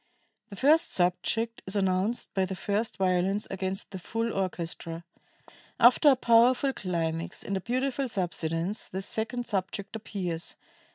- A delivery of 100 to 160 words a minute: Yes, slow, 135 wpm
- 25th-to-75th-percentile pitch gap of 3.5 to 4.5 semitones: Yes, average, 4.0 semitones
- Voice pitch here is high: Yes, high, 195 Hz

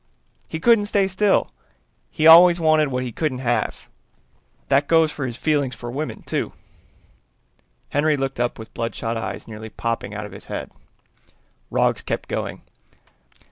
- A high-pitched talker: No, medium, 140 Hz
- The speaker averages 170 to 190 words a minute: No, average, 150 wpm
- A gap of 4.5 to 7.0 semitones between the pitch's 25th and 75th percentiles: Yes, wide, 5.4 semitones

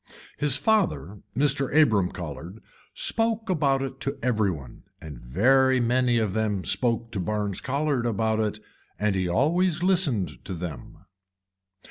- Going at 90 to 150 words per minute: Yes, average, 140 wpm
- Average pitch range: No, wide, 6.2 semitones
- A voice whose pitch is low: Yes, low, 115 Hz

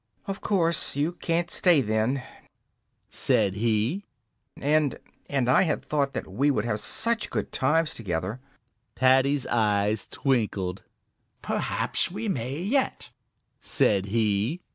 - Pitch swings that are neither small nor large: No, wide, 7.3 semitones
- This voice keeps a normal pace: No, slow, 120 wpm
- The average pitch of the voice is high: No, low, 135 Hz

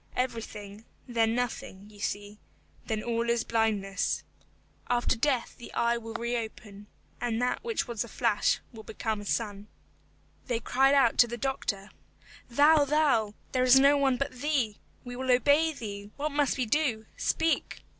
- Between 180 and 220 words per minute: No, average, 160 wpm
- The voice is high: Yes, high, 235 Hz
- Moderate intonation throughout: Yes, average, 3.6 semitones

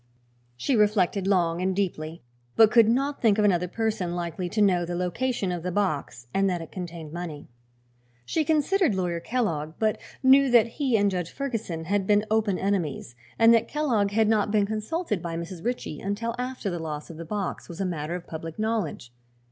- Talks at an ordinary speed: Yes, average, 195 wpm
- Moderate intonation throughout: Yes, average, 4.5 semitones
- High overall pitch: Yes, high, 195 Hz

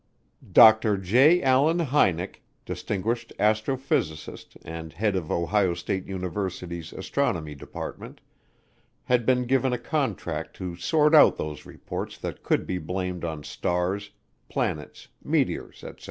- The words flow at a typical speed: No, slow, 125 wpm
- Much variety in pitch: Yes, wide, 6.2 semitones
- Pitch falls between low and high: No, low, 100 Hz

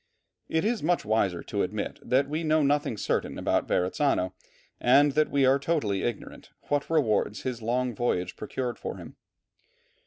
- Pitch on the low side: Yes, low, 130 Hz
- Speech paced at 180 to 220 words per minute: No, average, 155 wpm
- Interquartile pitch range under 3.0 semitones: No, average, 5.3 semitones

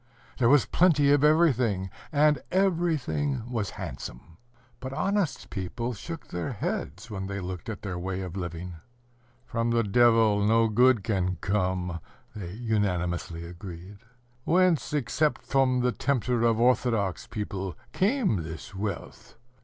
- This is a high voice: No, low, 110 Hz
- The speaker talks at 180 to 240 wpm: No, slow, 135 wpm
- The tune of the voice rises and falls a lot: Yes, wide, 6.2 semitones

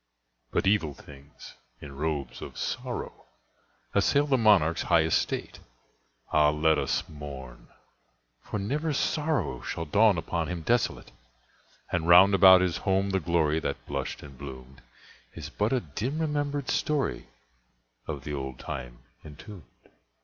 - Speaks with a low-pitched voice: Yes, very low, 80 Hz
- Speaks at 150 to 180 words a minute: No, slow, 135 wpm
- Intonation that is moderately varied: No, wide, 6.4 semitones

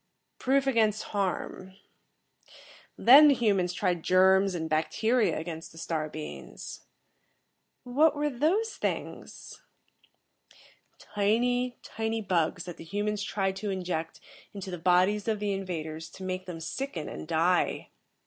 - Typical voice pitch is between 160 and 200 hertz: Yes, high, 190 Hz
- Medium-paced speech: No, slow, 130 wpm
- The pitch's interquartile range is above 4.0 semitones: Yes, average, 4.5 semitones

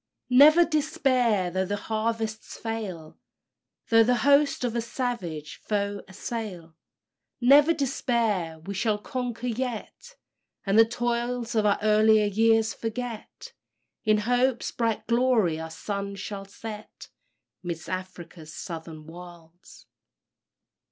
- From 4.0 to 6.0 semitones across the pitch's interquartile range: Yes, average, 4.4 semitones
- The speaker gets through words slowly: Yes, slow, 115 wpm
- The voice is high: Yes, high, 220 Hz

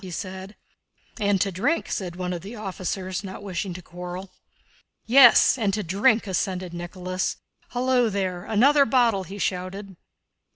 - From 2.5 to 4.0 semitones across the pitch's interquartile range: Yes, average, 2.9 semitones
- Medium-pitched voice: No, high, 195 Hz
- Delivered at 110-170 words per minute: Yes, average, 150 wpm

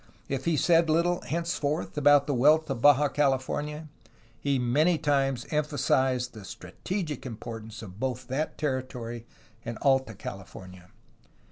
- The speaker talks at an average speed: No, slow, 130 wpm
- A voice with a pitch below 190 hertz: Yes, low, 135 Hz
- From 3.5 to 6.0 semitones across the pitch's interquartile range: Yes, average, 4.0 semitones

